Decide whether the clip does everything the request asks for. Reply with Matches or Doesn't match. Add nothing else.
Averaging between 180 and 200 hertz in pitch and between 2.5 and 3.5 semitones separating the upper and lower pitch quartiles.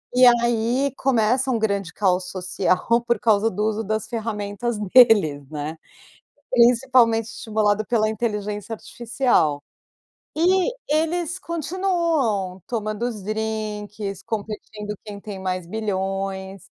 Doesn't match